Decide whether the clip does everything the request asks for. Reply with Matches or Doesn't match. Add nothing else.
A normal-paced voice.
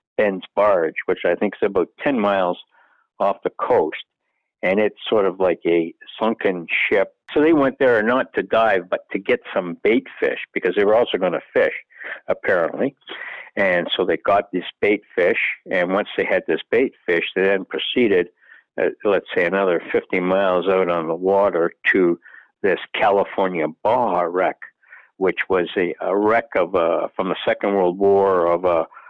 Matches